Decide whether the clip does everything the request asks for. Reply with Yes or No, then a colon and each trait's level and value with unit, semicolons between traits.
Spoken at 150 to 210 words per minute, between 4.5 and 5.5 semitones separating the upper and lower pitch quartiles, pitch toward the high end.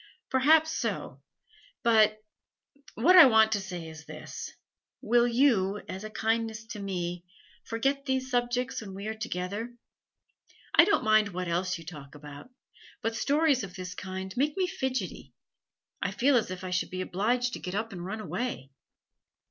Yes: average, 165 wpm; average, 5.0 semitones; high, 215 Hz